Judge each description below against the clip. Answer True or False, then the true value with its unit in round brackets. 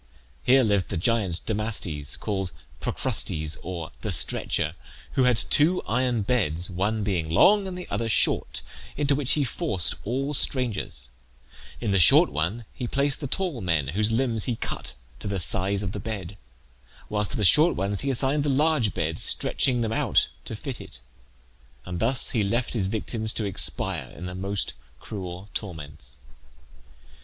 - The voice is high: False (105 Hz)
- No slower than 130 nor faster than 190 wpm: True (165 wpm)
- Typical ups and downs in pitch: False (5.7 semitones)